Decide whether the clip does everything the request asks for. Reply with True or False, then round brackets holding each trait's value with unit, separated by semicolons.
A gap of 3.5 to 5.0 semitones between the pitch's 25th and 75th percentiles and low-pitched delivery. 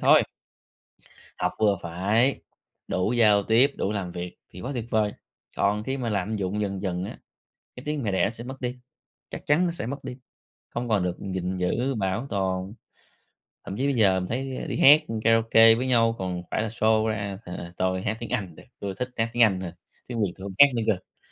True (4.3 semitones; 110 Hz)